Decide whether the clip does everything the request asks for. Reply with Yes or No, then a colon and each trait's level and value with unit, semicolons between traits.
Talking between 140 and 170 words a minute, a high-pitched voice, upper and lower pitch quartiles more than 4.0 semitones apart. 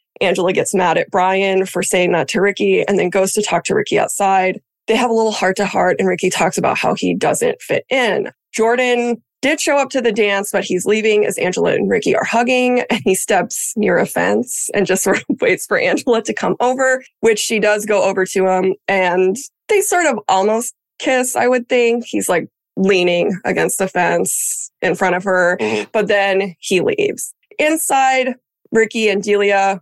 No: average, 200 wpm; high, 210 Hz; average, 4.5 semitones